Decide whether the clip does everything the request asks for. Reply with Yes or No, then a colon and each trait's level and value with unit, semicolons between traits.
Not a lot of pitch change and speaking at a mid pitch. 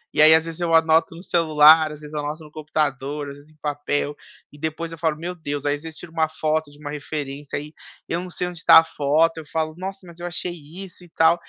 Yes: narrow, 2.0 semitones; medium, 155 Hz